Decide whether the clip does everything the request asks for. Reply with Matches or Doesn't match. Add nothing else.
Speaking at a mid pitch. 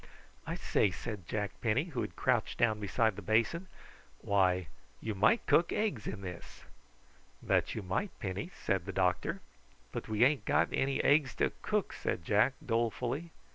Doesn't match